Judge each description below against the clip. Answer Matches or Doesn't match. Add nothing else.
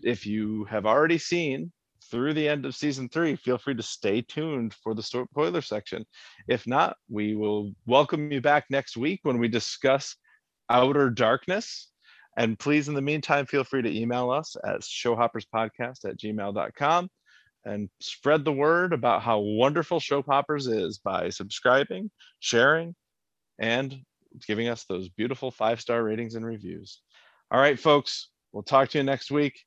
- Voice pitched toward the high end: Doesn't match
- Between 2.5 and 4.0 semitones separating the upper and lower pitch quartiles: Doesn't match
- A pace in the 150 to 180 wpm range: Matches